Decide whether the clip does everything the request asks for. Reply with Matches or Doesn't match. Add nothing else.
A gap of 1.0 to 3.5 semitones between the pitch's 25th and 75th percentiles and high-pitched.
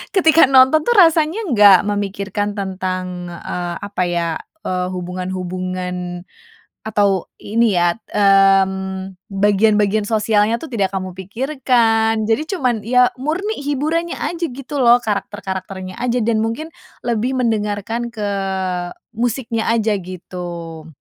Doesn't match